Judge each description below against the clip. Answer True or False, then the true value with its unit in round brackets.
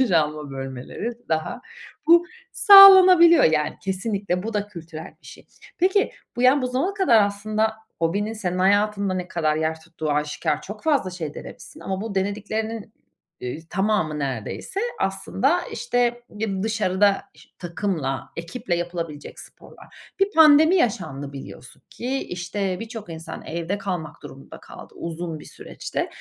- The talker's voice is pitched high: True (195 Hz)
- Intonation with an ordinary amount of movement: False (5.8 semitones)